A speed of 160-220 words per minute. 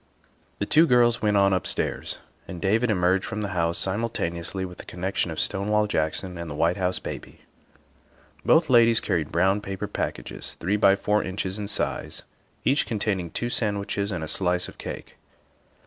Yes: average, 170 wpm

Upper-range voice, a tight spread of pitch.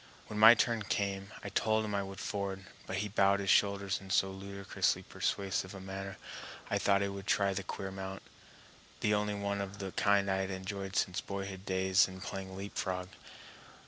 No: low, 100 Hz; narrow, 0.8 semitones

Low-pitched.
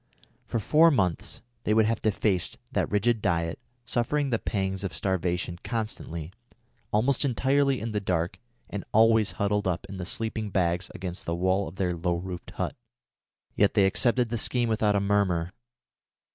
Yes: low, 100 Hz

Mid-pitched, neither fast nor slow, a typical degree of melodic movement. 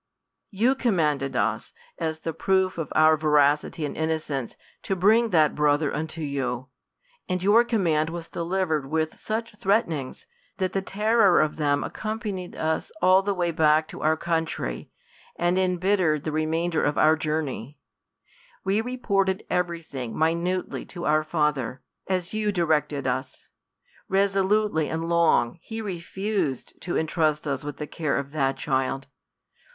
Yes: medium, 165 Hz; average, 150 wpm; average, 4.1 semitones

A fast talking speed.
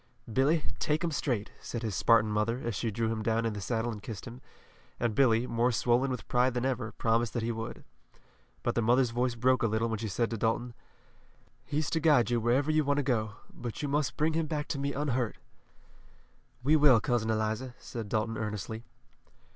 Yes: fast, 210 wpm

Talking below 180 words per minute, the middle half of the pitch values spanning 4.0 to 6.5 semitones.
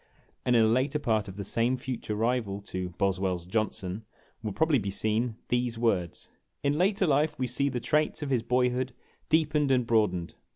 No: average, 190 wpm; average, 4.5 semitones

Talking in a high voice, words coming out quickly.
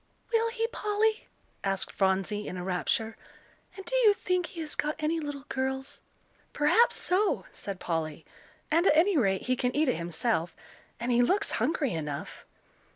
No: very high, 265 Hz; average, 165 wpm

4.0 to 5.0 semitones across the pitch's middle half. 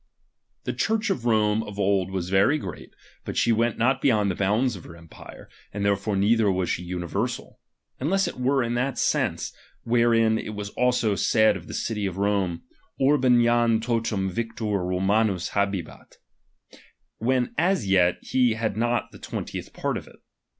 No: average, 3.5 semitones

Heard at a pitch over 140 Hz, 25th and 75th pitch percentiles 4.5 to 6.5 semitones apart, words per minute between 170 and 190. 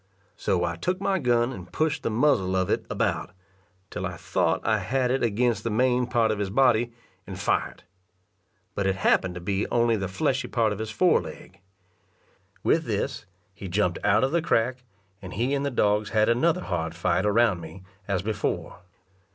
No: low, 110 Hz; average, 4.8 semitones; average, 185 wpm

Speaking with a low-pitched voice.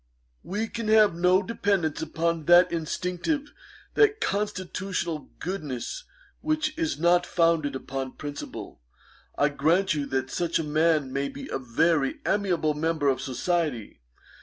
No: medium, 170 Hz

